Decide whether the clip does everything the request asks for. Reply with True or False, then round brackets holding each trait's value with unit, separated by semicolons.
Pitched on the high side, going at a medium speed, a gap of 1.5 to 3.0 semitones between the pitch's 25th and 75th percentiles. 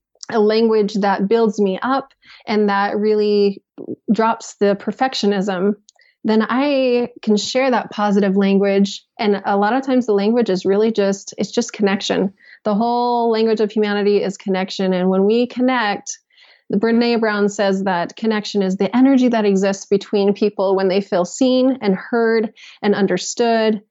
True (210 Hz; 160 wpm; 2.6 semitones)